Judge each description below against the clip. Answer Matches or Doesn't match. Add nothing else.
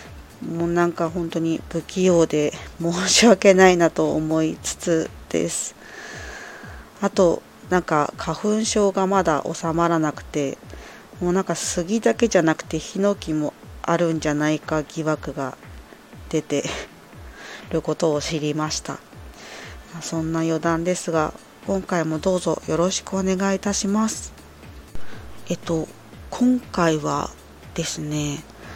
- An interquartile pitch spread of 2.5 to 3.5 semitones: Matches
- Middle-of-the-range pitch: Matches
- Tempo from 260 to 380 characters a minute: Doesn't match